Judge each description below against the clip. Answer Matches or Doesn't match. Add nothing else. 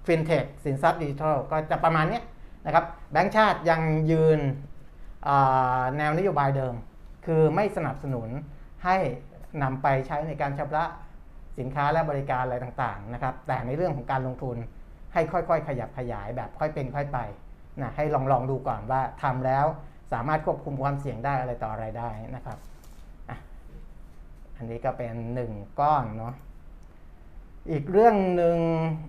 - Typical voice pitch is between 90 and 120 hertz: Doesn't match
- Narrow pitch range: Doesn't match